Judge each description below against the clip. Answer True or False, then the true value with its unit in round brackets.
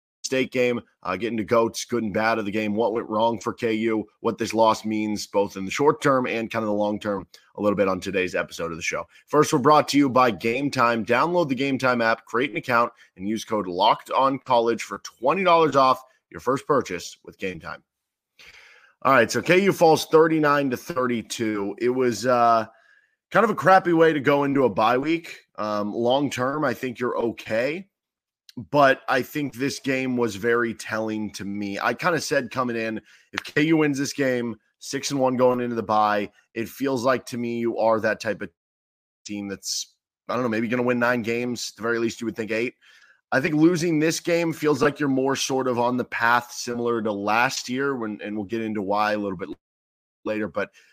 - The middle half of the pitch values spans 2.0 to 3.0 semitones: False (3.8 semitones)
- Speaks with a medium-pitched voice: False (120 Hz)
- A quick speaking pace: True (225 wpm)